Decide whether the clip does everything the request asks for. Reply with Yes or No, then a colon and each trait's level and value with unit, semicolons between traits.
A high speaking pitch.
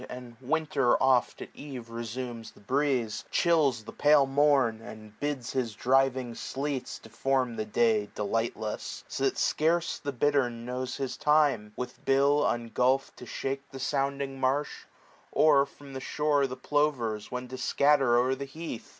No: low, 130 Hz